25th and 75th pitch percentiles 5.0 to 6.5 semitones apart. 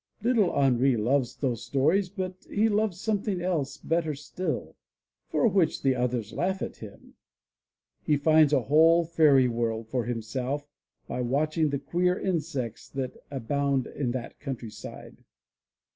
Yes: average, 5.3 semitones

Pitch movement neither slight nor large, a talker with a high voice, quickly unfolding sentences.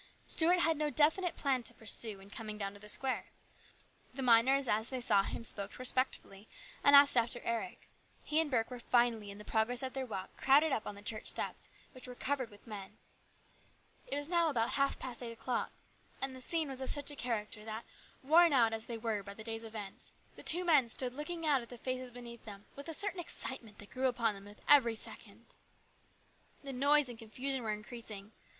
Yes: average, 4.1 semitones; high, 245 Hz; fast, 210 wpm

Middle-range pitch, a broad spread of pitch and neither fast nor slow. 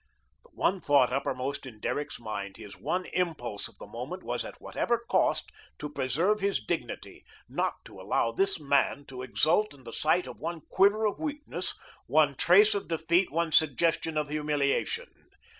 Yes: medium, 155 Hz; wide, 6.4 semitones; average, 170 wpm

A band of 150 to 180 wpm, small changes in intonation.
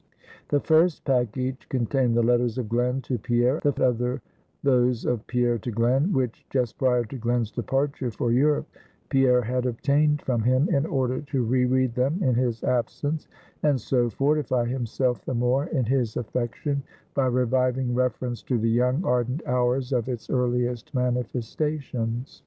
Yes: average, 160 wpm; narrow, 1.8 semitones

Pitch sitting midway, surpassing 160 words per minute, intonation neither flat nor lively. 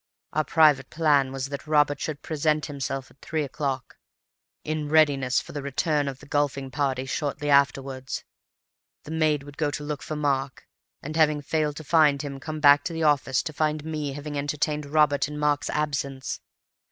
No: medium, 145 Hz; average, 175 wpm; narrow, 1.8 semitones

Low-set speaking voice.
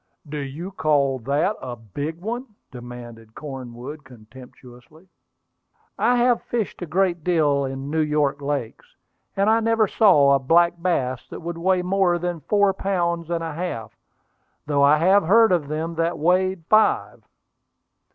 No: medium, 160 Hz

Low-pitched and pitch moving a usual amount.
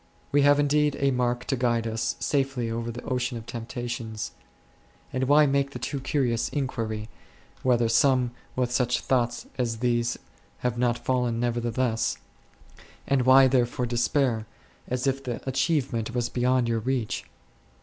No: low, 125 Hz; narrow, 2.2 semitones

